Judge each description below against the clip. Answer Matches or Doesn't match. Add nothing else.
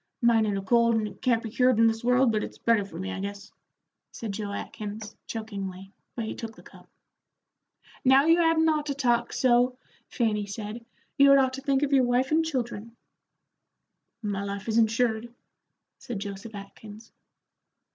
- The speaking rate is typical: Matches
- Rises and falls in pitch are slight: Doesn't match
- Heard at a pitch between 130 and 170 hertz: Doesn't match